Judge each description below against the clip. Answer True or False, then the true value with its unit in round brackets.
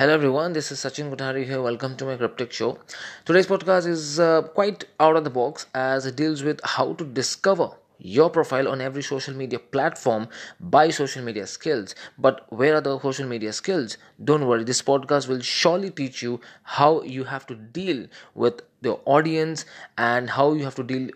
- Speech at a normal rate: True (195 wpm)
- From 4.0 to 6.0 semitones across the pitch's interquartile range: False (3.0 semitones)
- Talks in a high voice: False (135 Hz)